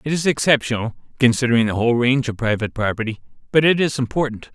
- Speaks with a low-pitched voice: Yes, low, 125 Hz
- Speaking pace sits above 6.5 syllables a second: Yes, 7.2 syllables/s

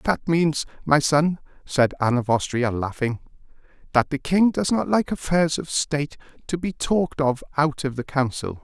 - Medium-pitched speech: Yes, medium, 150 Hz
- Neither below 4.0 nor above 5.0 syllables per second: Yes, 4.7 syllables/s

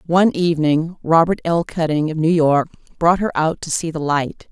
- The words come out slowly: No, average, 200 wpm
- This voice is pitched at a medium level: Yes, medium, 160 Hz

